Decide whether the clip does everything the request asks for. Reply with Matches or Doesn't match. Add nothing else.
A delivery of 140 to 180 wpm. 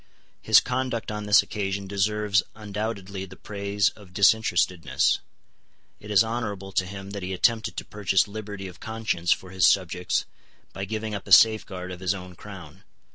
Matches